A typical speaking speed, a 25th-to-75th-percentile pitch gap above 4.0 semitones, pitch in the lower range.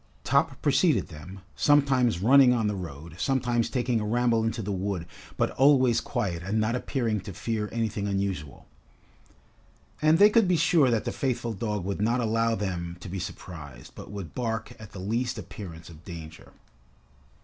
Yes: average, 170 wpm; average, 4.7 semitones; low, 110 Hz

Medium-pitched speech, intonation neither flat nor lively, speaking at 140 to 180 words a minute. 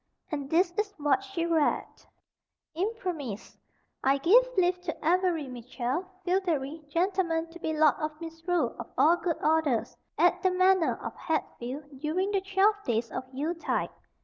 No: very high, 330 Hz; average, 3.9 semitones; average, 150 wpm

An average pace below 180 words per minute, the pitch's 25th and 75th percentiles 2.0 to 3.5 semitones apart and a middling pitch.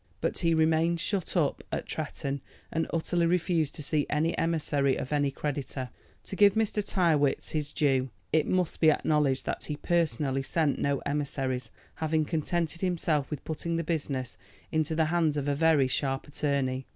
Yes: average, 170 wpm; average, 2.9 semitones; medium, 155 Hz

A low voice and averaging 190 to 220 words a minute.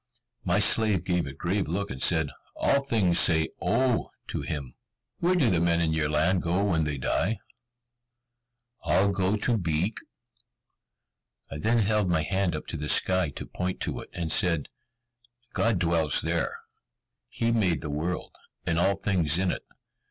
No: very low, 90 Hz; average, 165 wpm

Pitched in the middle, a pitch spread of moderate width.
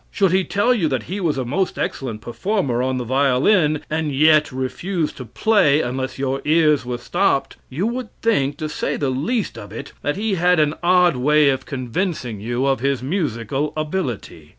No: medium, 145 Hz; wide, 5.7 semitones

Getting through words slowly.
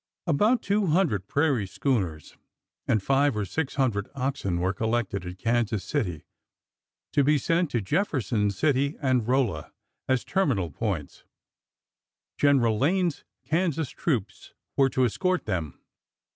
Yes: slow, 130 wpm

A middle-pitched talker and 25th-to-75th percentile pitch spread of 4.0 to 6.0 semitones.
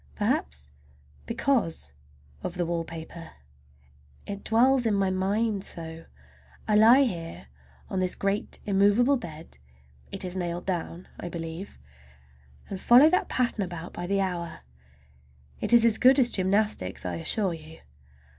Yes: medium, 180 Hz; average, 4.9 semitones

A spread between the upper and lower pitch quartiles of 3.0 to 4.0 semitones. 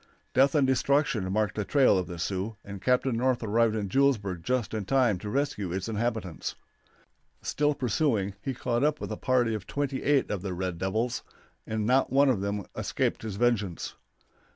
No: average, 4.8 semitones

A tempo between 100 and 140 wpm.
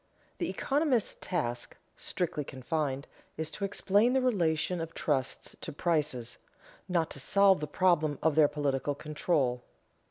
Yes: slow, 135 wpm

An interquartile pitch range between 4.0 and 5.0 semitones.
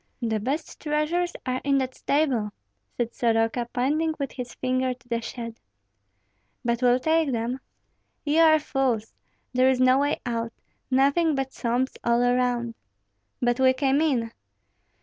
No: average, 3.0 semitones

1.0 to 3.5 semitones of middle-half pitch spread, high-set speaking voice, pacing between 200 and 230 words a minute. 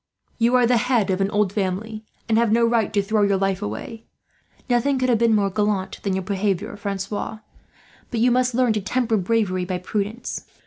Yes: average, 3.0 semitones; high, 215 Hz; fast, 205 wpm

